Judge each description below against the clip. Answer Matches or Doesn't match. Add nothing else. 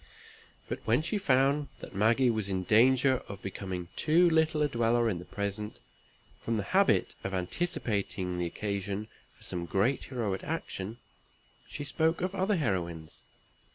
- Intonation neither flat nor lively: Doesn't match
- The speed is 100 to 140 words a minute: Doesn't match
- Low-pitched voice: Matches